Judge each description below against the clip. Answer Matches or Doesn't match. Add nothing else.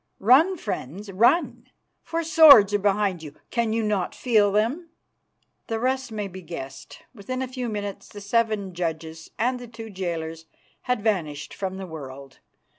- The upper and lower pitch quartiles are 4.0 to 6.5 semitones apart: Matches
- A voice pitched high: Matches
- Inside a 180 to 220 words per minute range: Doesn't match